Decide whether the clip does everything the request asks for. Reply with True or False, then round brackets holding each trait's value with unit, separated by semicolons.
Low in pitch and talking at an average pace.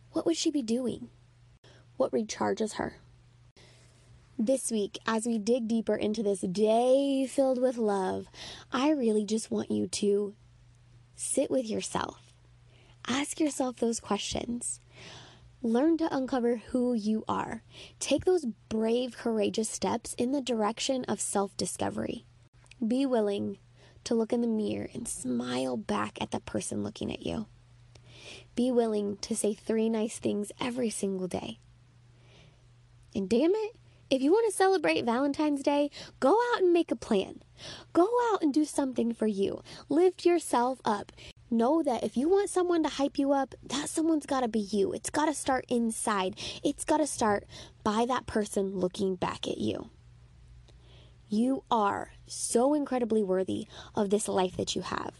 False (220 Hz; 160 wpm)